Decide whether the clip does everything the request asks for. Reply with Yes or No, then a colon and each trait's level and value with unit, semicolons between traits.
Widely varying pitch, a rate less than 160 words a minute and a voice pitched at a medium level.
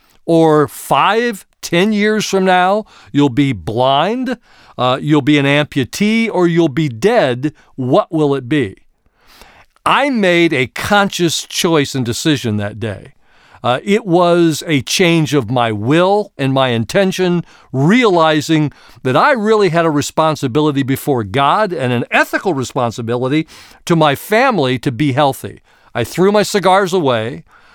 Yes: wide, 5.9 semitones; average, 145 wpm; medium, 155 Hz